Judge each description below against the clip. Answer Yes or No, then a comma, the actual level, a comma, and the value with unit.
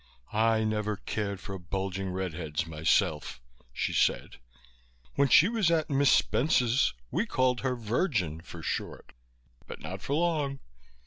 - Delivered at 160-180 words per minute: No, average, 140 wpm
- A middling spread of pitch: No, wide, 7.1 semitones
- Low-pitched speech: Yes, low, 105 Hz